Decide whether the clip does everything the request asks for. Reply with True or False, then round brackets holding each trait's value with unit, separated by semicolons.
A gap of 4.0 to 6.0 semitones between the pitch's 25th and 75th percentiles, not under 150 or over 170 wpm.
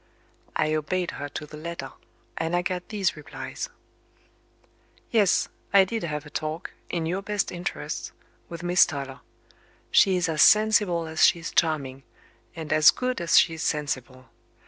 False (3.1 semitones; 160 wpm)